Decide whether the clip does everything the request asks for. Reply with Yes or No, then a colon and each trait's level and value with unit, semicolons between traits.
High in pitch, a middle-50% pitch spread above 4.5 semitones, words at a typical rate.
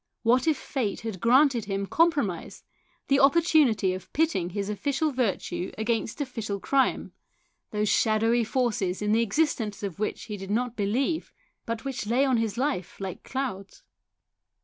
Yes: high, 230 Hz; average, 4.9 semitones; average, 150 wpm